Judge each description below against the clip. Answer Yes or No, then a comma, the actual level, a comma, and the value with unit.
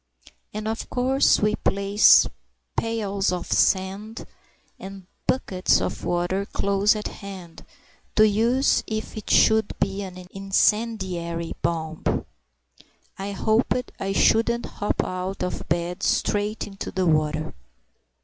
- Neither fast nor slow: No, slow, 120 wpm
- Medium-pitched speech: No, high, 195 Hz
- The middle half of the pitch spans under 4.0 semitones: Yes, average, 2.9 semitones